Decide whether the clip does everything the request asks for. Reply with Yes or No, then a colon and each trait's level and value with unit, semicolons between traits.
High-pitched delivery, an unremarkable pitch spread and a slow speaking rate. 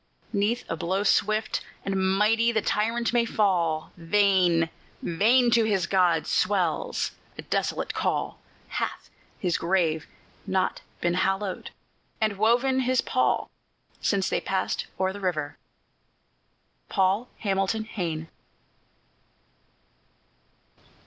Yes: high, 195 Hz; average, 3.6 semitones; slow, 110 wpm